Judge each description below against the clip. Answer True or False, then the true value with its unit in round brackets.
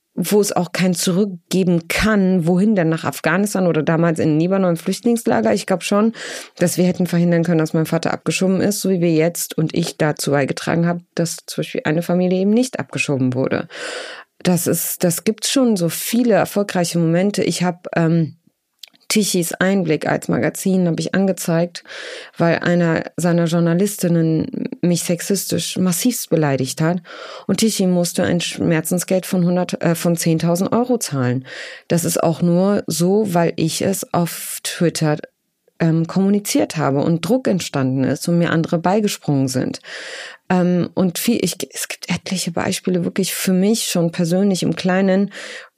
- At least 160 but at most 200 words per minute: True (165 wpm)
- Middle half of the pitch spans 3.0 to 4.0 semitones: False (2.5 semitones)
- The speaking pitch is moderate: True (175 Hz)